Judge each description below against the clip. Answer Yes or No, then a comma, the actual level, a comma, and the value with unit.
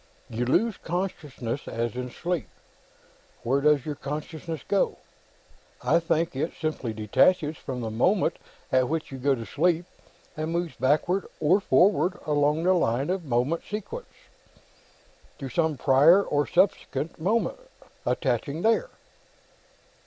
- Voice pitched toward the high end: No, medium, 155 Hz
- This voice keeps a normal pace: No, slow, 130 wpm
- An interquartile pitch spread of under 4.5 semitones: No, average, 4.8 semitones